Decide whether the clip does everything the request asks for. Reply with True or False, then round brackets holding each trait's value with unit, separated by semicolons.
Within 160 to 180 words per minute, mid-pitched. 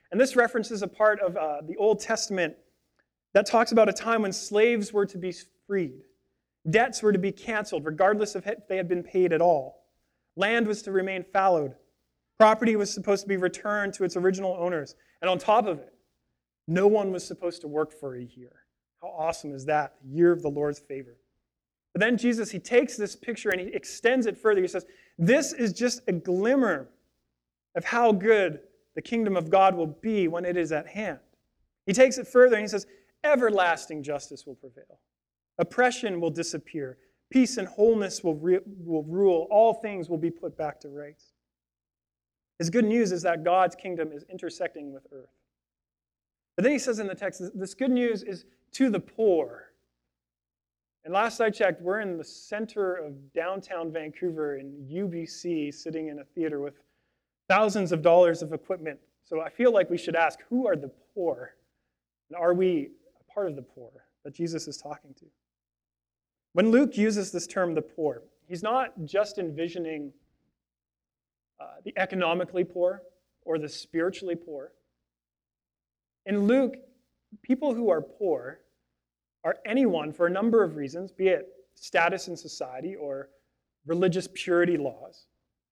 True (175 wpm; 175 Hz)